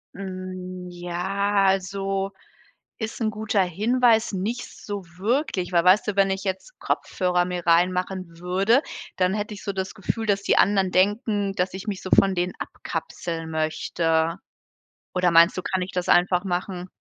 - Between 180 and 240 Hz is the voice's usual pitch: Yes, high, 190 Hz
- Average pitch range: No, narrow, 2.1 semitones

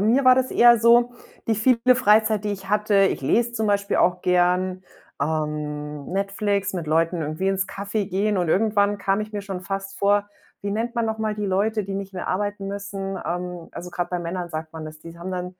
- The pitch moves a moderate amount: Yes, average, 3.0 semitones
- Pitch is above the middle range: Yes, high, 195 Hz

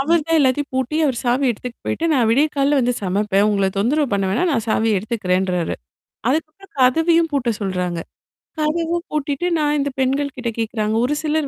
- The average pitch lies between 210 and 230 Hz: No, very high, 260 Hz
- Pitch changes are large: Yes, wide, 5.9 semitones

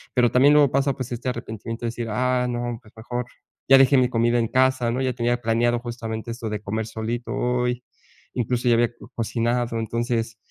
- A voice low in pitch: Yes, low, 120 Hz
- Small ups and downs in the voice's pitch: Yes, narrow, 1.5 semitones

